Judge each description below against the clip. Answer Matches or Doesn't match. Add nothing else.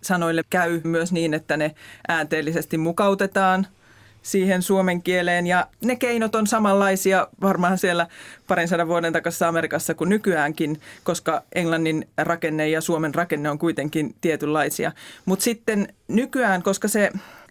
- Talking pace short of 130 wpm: Doesn't match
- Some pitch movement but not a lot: Matches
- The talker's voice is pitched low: Doesn't match